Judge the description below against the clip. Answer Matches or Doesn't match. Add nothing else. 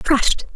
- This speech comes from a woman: Matches